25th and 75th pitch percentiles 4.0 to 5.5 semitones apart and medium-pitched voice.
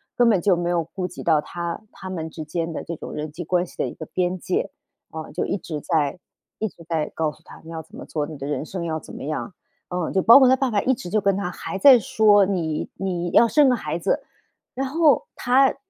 Yes: average, 4.8 semitones; medium, 180 Hz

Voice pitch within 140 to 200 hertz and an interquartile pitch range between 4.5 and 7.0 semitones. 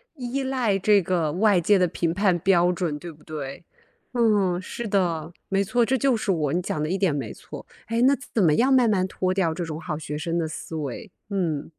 Yes: medium, 185 Hz; average, 4.8 semitones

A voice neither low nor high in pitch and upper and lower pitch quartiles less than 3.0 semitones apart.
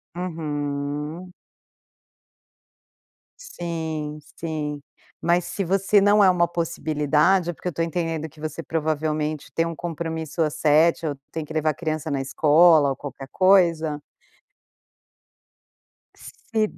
Yes: medium, 160 Hz; narrow, 2.4 semitones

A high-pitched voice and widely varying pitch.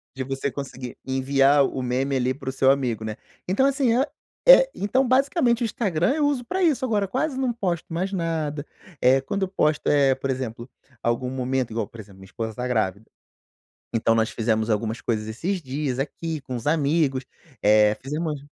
No: low, 135 Hz; wide, 7.5 semitones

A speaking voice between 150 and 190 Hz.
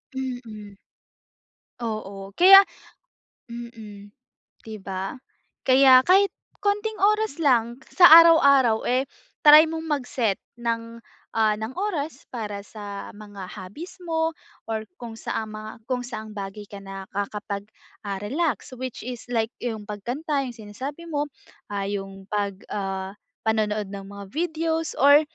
No: high, 230 Hz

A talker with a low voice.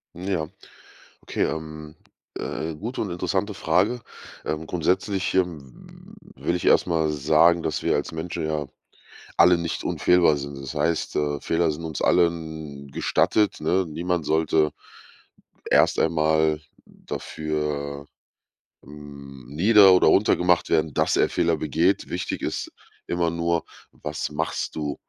Yes: very low, 80 Hz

